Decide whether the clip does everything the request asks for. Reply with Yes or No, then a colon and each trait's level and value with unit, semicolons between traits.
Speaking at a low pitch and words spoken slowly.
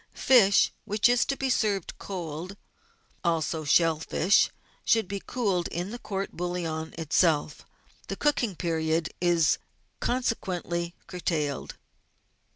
No: medium, 175 Hz; slow, 115 wpm